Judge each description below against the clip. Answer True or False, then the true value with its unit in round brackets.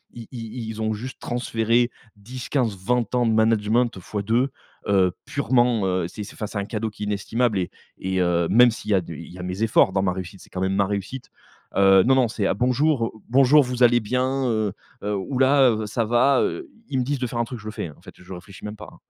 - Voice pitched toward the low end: True (110 Hz)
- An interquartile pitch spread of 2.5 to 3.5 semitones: False (4.0 semitones)